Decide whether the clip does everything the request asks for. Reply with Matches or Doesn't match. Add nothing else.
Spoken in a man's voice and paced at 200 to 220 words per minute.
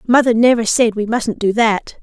Doesn't match